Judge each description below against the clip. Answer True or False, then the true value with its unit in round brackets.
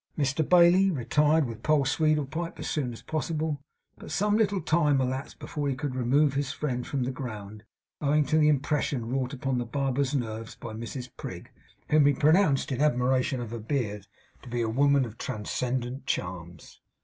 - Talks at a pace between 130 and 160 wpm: False (180 wpm)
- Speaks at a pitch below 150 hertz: True (135 Hz)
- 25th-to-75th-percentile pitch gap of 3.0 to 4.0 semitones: True (3.7 semitones)